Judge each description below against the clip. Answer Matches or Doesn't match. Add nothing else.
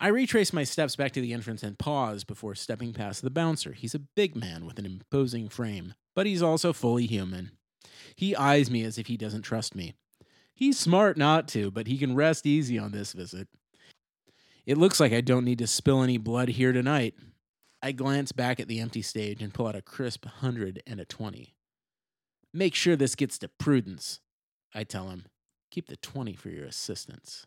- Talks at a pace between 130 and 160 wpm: Doesn't match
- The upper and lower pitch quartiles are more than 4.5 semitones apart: Matches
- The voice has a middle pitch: Doesn't match